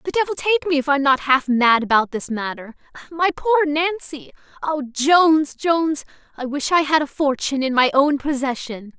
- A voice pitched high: Yes, very high, 290 Hz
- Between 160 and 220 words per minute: Yes, average, 195 wpm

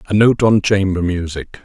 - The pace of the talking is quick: No, average, 185 wpm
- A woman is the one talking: No, male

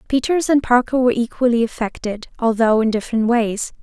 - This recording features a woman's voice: Yes, female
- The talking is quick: No, average, 155 wpm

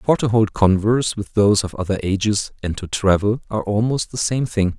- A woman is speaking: No, male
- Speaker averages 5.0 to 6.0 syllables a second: Yes, 5.5 syllables/s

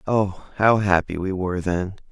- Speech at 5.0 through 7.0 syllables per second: No, 4.6 syllables/s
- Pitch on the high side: No, very low, 95 Hz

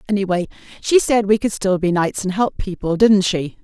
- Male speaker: No, female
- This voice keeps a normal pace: No, fast, 215 wpm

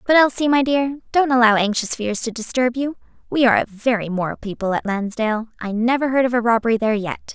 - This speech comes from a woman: Yes, female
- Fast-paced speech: Yes, fast, 220 wpm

